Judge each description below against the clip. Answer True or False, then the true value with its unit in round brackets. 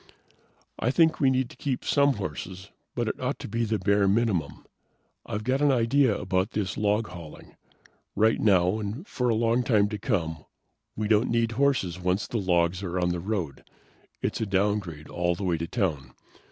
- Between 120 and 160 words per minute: False (190 wpm)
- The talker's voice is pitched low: True (105 Hz)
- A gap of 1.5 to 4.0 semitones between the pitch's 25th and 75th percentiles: False (4.4 semitones)